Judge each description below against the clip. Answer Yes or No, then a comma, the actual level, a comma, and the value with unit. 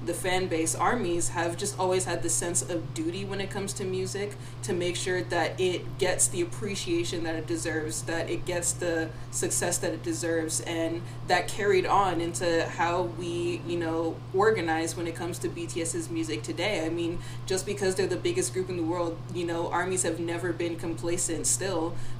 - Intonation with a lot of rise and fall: Yes, wide, 6.0 semitones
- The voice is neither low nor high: Yes, medium, 165 Hz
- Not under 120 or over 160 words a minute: No, average, 195 wpm